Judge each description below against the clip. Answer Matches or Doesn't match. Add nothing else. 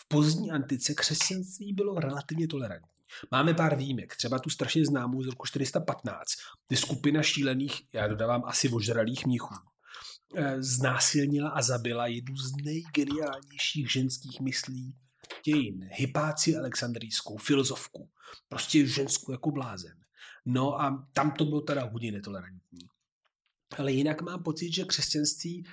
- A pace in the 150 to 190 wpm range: Doesn't match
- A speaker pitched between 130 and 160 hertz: Matches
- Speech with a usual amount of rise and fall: Matches